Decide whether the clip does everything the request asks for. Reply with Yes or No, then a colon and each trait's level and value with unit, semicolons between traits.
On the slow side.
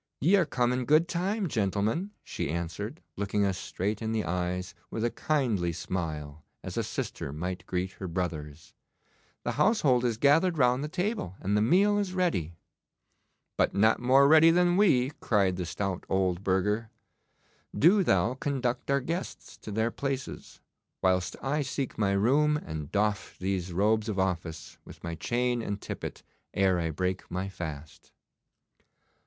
No: average, 160 wpm